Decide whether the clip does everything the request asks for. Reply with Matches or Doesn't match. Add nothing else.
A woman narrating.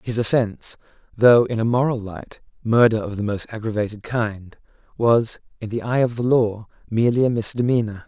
Doesn't match